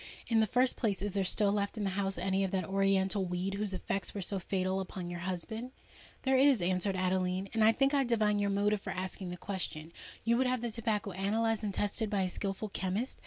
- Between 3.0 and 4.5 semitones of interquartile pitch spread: No, narrow, 2.6 semitones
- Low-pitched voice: No, high, 200 Hz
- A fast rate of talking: Yes, fast, 230 wpm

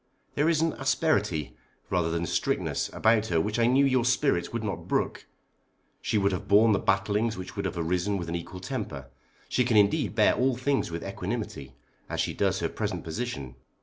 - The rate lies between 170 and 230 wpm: Yes, average, 195 wpm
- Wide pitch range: Yes, wide, 6.1 semitones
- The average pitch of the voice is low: Yes, low, 105 Hz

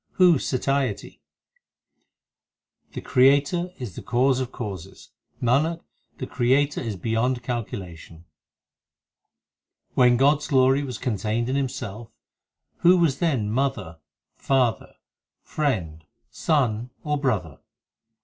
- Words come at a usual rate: No, slow, 110 wpm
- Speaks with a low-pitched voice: Yes, low, 125 Hz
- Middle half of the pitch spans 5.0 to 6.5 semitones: No, average, 4.2 semitones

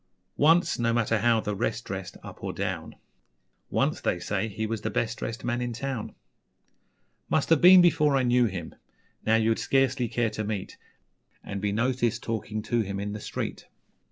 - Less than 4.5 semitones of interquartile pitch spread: Yes, average, 2.8 semitones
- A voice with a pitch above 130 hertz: No, low, 115 Hz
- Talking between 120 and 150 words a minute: No, average, 185 wpm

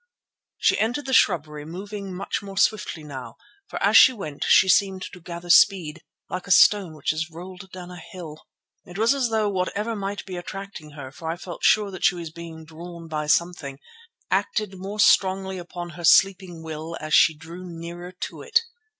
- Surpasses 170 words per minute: Yes, average, 190 wpm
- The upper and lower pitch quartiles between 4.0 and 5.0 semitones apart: No, average, 3.3 semitones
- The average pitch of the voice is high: No, medium, 180 Hz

